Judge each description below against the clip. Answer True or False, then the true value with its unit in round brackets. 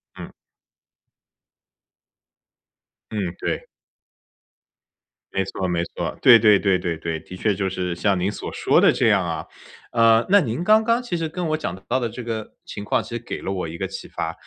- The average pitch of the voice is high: False (105 Hz)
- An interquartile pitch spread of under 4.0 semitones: False (5.5 semitones)